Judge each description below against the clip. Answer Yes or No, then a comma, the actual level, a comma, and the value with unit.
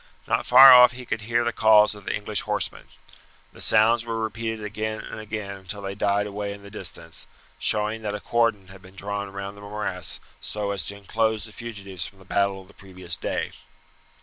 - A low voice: Yes, low, 105 Hz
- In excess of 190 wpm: Yes, fast, 205 wpm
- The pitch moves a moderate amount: No, narrow, 2.0 semitones